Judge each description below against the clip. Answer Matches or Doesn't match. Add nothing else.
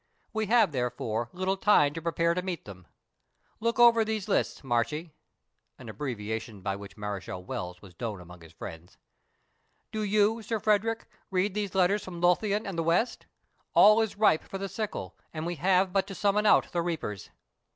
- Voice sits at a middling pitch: Matches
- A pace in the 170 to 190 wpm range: Matches